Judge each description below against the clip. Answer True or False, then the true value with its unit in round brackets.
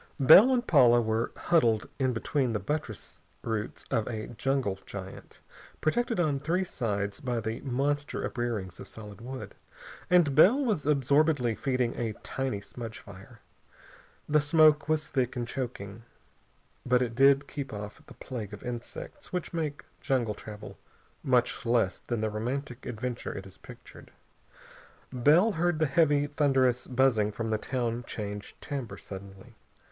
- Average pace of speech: True (150 wpm)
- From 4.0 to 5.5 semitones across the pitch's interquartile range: True (4.7 semitones)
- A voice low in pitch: True (125 Hz)